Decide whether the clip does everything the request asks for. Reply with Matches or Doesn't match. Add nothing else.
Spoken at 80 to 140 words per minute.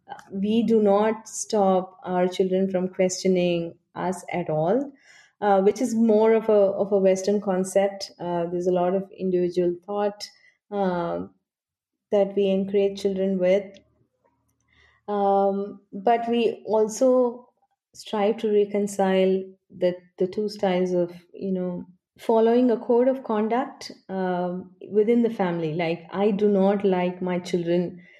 Matches